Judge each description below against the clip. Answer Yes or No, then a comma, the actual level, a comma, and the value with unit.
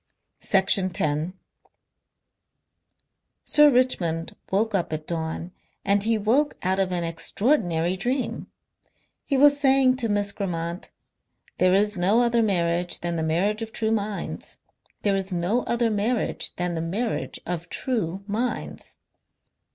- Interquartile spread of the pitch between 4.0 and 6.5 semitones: Yes, average, 4.9 semitones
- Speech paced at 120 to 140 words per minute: Yes, slow, 135 wpm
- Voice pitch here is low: No, high, 200 Hz